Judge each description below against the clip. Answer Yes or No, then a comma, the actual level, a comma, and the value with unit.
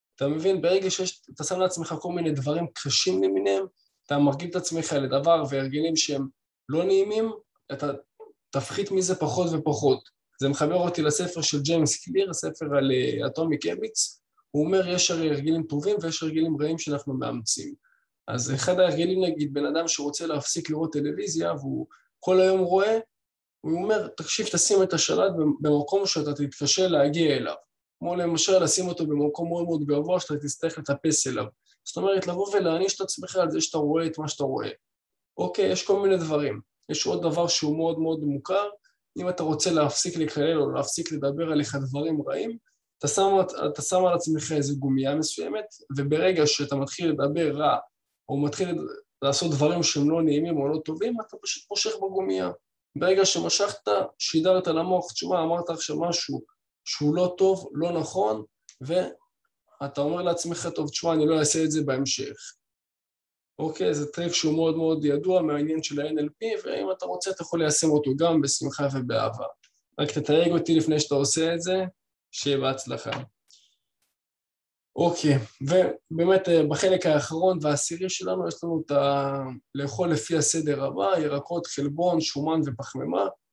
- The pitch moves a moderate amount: Yes, average, 3.8 semitones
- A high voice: No, medium, 160 Hz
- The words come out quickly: Yes, fast, 160 wpm